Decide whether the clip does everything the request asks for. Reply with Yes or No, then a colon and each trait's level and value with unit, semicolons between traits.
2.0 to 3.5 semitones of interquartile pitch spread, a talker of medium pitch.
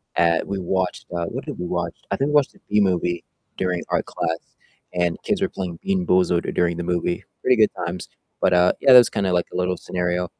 No: narrow, 2.6 semitones; very low, 90 Hz